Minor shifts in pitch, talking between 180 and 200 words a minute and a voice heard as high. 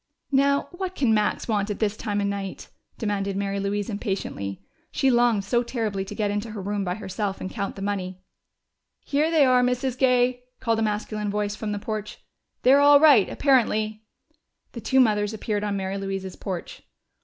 No: average, 3.7 semitones; average, 185 wpm; high, 210 Hz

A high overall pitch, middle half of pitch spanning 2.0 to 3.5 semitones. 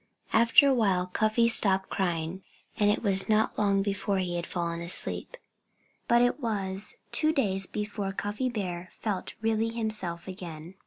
Yes: high, 200 Hz; average, 3.2 semitones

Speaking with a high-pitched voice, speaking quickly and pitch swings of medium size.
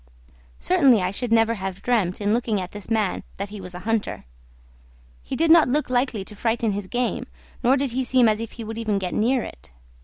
Yes: high, 225 Hz; fast, 220 wpm; average, 3.6 semitones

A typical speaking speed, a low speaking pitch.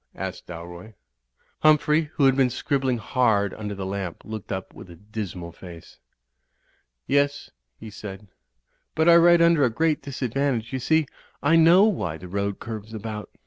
Yes: average, 165 wpm; low, 115 Hz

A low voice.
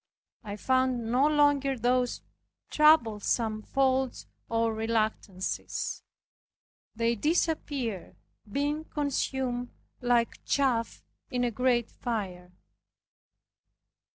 No: high, 245 Hz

